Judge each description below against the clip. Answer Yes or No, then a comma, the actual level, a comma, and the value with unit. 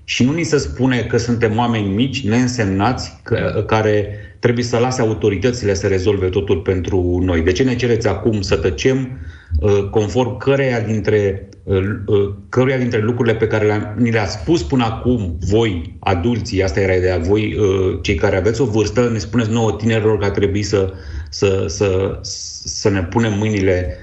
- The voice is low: Yes, low, 105 Hz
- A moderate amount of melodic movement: Yes, average, 3.6 semitones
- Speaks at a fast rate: Yes, fast, 175 wpm